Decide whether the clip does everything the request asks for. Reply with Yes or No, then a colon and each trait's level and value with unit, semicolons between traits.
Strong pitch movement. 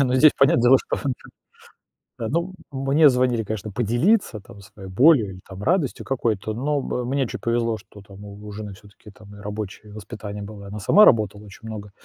No: average, 4.2 semitones